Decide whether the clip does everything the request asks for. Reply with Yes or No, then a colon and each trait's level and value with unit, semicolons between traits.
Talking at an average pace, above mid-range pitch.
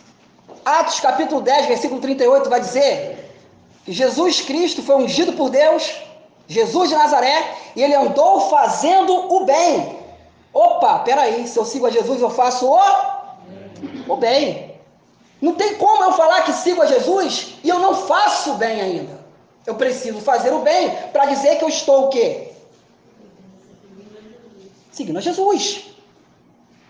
Yes: average, 145 wpm; very high, 305 Hz